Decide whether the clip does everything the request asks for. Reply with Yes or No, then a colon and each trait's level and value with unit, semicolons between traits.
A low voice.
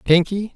No: medium, 185 Hz